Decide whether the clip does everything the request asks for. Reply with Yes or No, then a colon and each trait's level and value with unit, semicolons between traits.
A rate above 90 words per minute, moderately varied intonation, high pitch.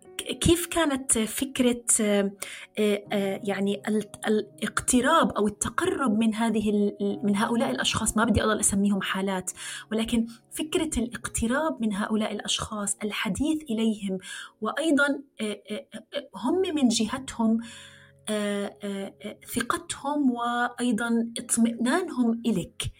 No: average, 85 wpm; average, 3.3 semitones; high, 225 Hz